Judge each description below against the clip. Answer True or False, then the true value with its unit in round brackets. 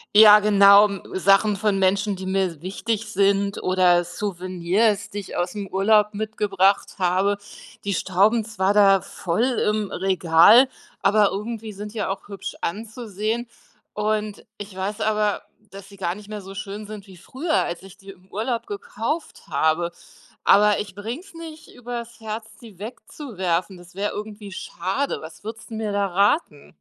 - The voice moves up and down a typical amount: False (2.3 semitones)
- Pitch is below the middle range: False (205 Hz)